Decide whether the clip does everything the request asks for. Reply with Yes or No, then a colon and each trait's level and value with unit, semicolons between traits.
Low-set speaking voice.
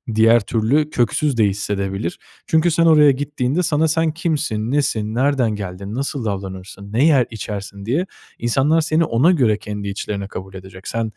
Yes: low, 115 Hz